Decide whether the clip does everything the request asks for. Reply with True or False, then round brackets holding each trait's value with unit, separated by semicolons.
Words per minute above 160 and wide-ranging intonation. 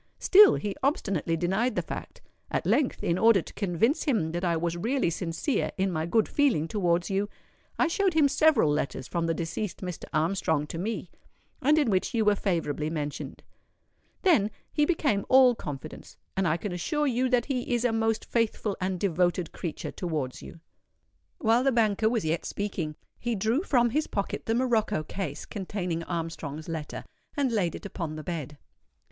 True (180 wpm; 6.4 semitones)